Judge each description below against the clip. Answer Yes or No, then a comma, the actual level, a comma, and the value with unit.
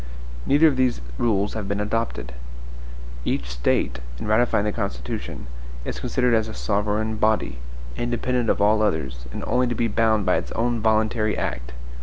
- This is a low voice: Yes, low, 110 Hz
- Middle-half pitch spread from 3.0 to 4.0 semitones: No, narrow, 2.6 semitones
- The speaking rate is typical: Yes, average, 165 wpm